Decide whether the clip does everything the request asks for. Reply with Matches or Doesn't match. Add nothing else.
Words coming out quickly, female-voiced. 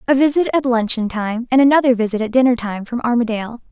Matches